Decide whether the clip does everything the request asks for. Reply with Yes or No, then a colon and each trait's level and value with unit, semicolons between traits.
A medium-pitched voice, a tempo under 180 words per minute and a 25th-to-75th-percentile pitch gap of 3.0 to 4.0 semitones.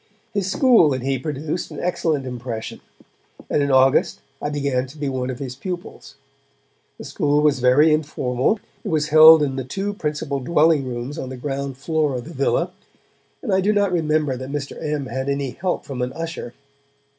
No: medium, 145 Hz; average, 190 wpm; average, 3.5 semitones